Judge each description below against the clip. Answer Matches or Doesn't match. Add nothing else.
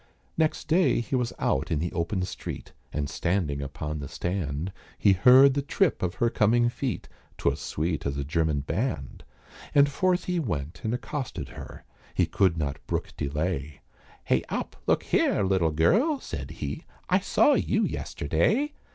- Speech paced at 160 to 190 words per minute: Matches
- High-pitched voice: Doesn't match